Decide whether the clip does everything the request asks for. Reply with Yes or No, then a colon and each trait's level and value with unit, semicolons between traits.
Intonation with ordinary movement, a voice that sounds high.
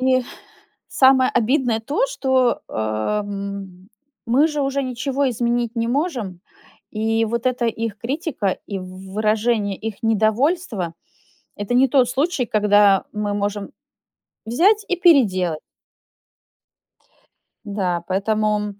Yes: average, 4.3 semitones; high, 225 Hz